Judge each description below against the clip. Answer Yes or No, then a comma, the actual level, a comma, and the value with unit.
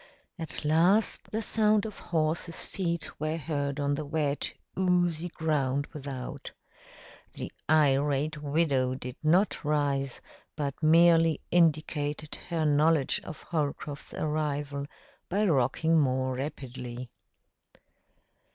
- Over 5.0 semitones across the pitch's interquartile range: No, average, 2.7 semitones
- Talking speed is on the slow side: Yes, slow, 105 wpm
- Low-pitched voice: No, medium, 150 Hz